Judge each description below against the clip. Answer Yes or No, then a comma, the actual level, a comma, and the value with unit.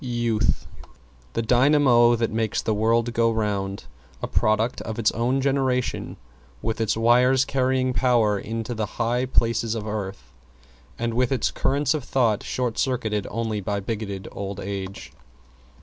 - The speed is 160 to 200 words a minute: No, average, 150 wpm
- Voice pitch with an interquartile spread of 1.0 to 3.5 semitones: Yes, average, 2.8 semitones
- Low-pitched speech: Yes, low, 115 Hz